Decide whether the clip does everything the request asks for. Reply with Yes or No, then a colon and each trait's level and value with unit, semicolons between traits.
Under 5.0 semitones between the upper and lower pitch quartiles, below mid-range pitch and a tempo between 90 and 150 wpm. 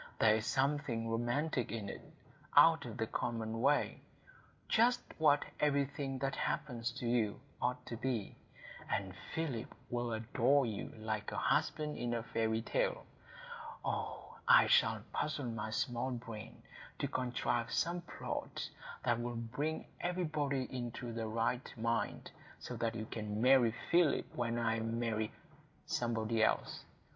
Yes: average, 3.7 semitones; low, 120 Hz; slow, 135 wpm